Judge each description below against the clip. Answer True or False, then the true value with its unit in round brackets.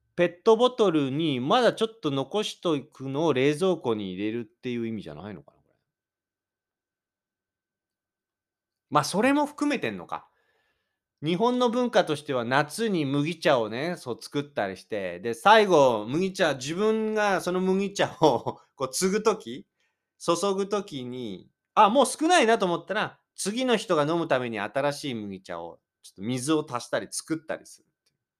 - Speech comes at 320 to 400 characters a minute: False (290 characters per minute)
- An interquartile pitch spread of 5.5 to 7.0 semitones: False (8.0 semitones)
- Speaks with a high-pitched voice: False (170 Hz)